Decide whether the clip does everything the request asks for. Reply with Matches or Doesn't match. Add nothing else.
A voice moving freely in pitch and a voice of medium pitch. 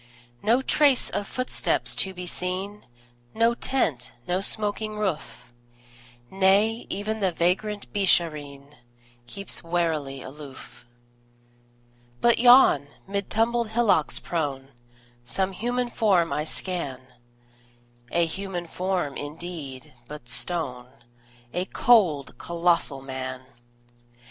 Matches